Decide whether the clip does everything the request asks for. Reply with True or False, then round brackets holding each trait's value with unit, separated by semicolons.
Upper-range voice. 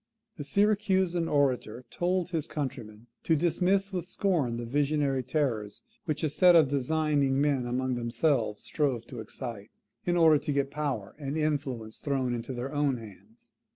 False (140 Hz)